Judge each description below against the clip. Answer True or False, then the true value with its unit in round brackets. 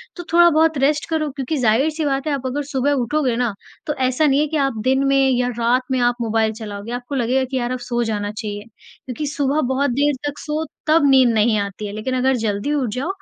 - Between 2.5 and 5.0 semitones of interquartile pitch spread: True (3.5 semitones)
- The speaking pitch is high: True (260 Hz)